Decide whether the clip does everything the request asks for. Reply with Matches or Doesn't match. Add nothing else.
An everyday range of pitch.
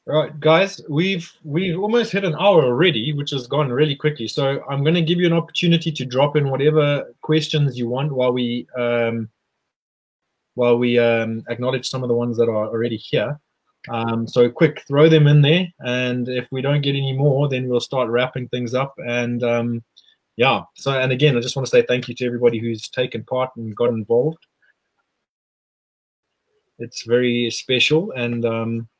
Matches